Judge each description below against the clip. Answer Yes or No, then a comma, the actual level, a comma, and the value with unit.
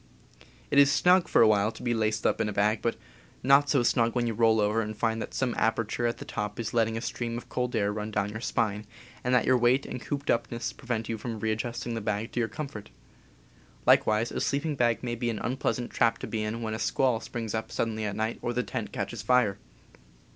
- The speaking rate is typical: No, fast, 245 wpm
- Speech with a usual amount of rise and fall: No, narrow, 2.0 semitones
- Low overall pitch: Yes, low, 115 Hz